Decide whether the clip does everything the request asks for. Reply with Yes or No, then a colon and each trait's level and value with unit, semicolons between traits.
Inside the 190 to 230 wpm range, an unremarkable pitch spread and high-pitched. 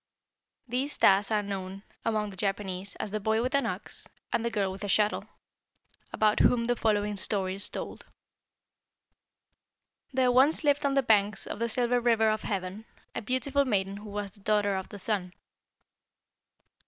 No: average, 170 wpm; average, 3.2 semitones; high, 210 Hz